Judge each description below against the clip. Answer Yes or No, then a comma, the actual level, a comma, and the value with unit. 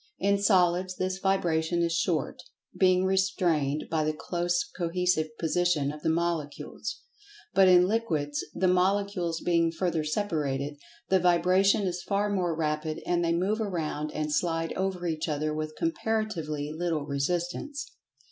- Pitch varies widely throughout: No, average, 3.3 semitones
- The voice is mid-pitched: Yes, medium, 175 Hz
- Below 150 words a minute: Yes, average, 140 wpm